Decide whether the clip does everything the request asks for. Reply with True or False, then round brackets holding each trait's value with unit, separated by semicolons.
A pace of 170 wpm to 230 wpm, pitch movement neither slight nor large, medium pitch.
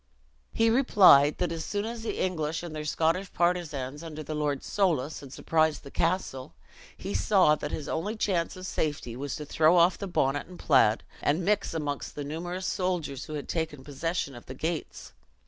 True (185 wpm; 3.9 semitones; 160 Hz)